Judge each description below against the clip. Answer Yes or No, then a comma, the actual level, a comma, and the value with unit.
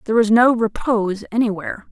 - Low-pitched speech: No, high, 220 Hz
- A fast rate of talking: No, average, 155 wpm